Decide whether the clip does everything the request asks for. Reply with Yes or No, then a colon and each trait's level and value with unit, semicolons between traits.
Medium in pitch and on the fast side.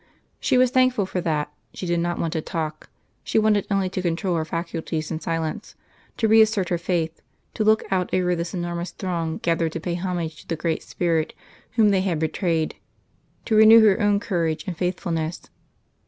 No: medium, 175 Hz; average, 185 wpm